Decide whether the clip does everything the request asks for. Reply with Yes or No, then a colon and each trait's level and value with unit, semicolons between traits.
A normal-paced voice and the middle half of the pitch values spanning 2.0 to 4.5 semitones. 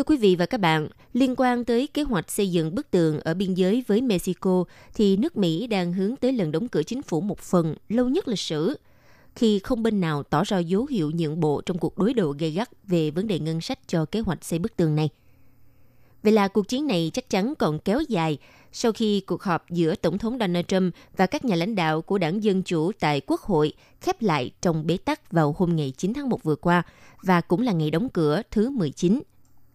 No: average, 235 wpm; average, 5.2 semitones